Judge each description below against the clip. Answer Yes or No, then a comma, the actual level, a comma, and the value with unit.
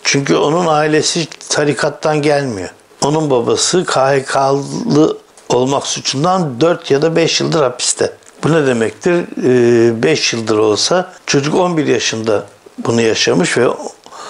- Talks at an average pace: Yes, average, 115 wpm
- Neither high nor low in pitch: Yes, medium, 150 Hz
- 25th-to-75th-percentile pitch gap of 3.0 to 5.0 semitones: Yes, average, 4.0 semitones